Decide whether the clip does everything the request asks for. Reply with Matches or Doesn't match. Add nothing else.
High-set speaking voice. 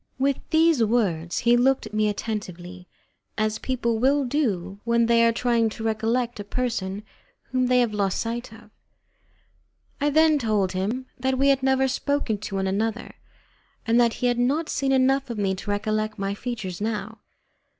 Matches